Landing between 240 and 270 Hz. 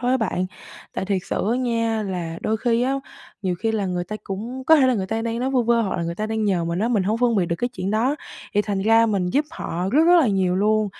No: high, 215 Hz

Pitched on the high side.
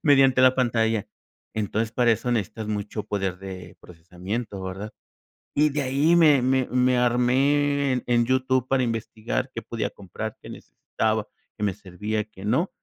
No: low, 115 Hz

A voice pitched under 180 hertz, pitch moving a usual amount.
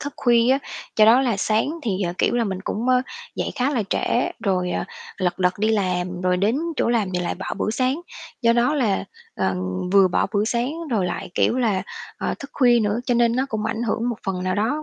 No: high, 220 Hz; average, 4.5 semitones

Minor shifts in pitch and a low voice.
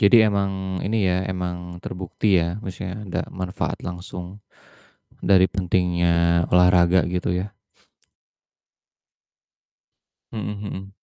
Yes: narrow, 1.7 semitones; very low, 90 Hz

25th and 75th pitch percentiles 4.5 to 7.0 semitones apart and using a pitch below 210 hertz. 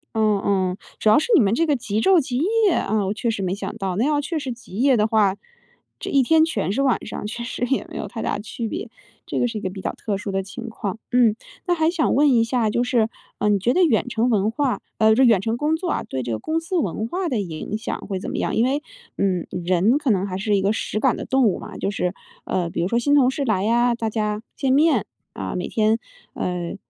No: average, 5.1 semitones; high, 225 Hz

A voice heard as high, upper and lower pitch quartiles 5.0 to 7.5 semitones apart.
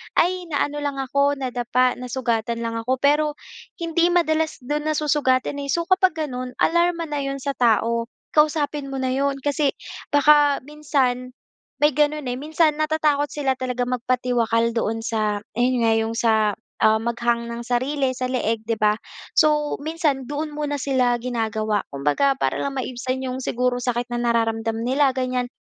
No: very high, 260 Hz; average, 3.8 semitones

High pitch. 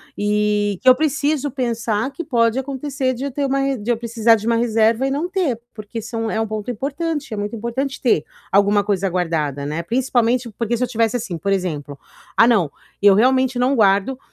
Yes: high, 230 Hz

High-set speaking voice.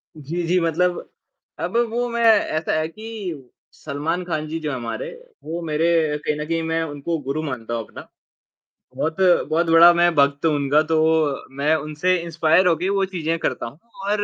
No: medium, 160 Hz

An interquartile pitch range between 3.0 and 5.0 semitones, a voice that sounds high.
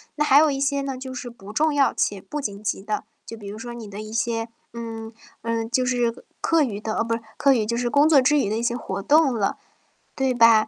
Yes: average, 3.6 semitones; high, 235 Hz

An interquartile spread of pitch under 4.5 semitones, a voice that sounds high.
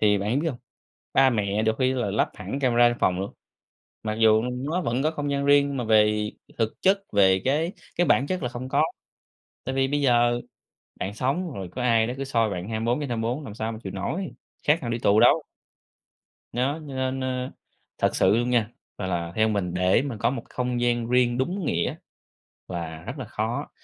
No: average, 3.9 semitones; low, 120 Hz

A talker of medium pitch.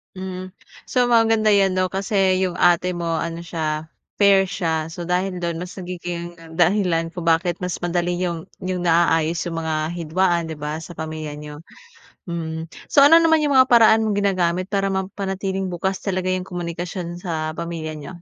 Yes: medium, 175 Hz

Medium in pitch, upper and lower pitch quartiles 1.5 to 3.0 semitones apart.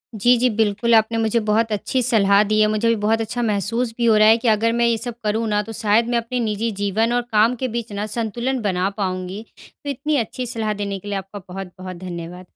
No: high, 220 Hz; narrow, 2.5 semitones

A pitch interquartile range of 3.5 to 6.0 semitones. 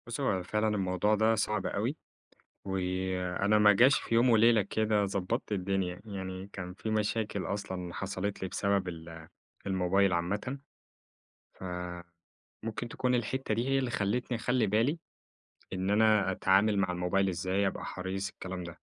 No: average, 2.8 semitones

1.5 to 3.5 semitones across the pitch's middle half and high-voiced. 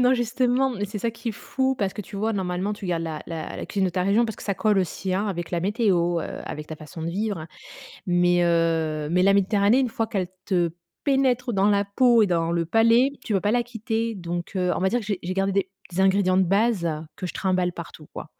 No: average, 4.2 semitones; high, 195 Hz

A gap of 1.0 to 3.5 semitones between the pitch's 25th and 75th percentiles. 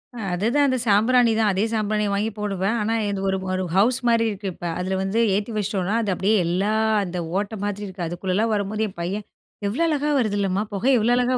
Yes: average, 2.8 semitones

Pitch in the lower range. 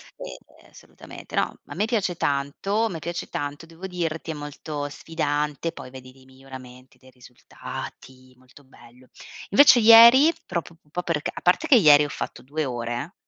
No: medium, 150 Hz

